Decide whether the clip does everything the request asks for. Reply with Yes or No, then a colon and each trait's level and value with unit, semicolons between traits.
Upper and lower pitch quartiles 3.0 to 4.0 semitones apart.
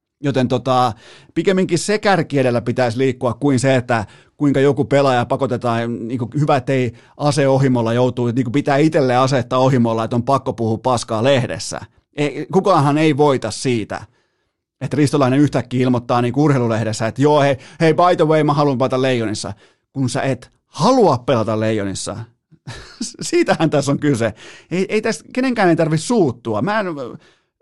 Yes: average, 3.5 semitones